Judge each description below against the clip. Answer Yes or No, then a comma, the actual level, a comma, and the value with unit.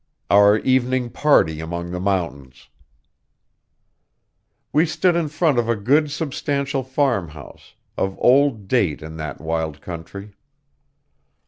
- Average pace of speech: No, slow, 115 wpm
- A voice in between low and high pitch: No, low, 105 Hz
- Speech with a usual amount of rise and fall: No, wide, 9.0 semitones